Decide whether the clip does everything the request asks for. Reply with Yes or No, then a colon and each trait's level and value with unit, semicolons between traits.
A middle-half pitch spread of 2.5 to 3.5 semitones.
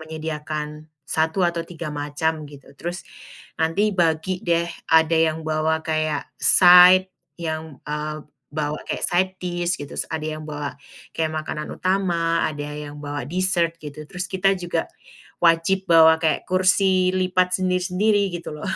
Yes: average, 2.8 semitones